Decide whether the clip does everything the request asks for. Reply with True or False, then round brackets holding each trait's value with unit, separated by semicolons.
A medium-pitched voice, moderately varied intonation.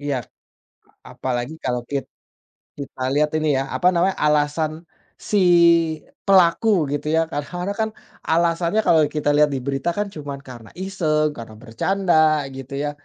True (150 Hz; 3.8 semitones)